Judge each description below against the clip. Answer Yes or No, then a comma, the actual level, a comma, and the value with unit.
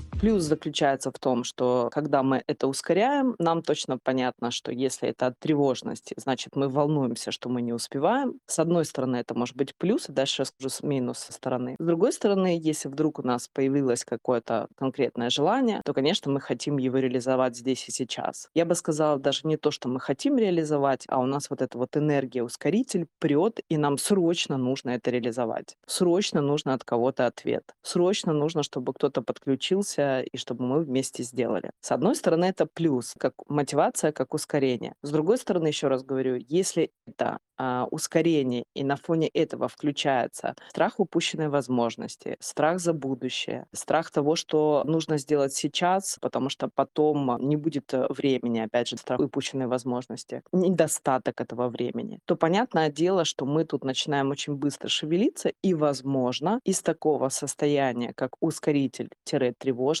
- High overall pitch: No, medium, 140 Hz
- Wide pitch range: No, average, 3.7 semitones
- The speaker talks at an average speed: No, fast, 170 wpm